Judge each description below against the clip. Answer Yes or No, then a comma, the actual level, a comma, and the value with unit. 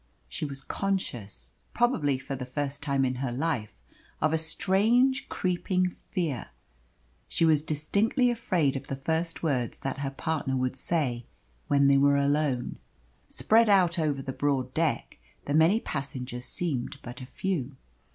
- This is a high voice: No, medium, 145 Hz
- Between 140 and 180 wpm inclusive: Yes, average, 150 wpm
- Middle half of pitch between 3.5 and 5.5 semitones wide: Yes, average, 4.6 semitones